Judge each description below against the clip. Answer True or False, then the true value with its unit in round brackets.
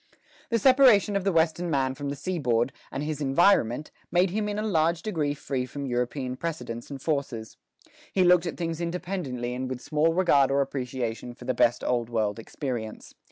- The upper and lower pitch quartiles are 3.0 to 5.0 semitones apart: False (5.6 semitones)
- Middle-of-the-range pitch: True (145 Hz)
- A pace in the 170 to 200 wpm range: True (185 wpm)